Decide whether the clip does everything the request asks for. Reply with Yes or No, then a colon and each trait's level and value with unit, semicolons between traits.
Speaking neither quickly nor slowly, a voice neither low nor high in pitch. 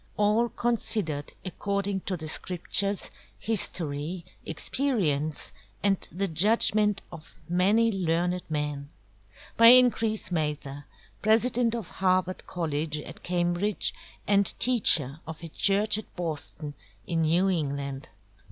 No: slow, 110 wpm; medium, 180 Hz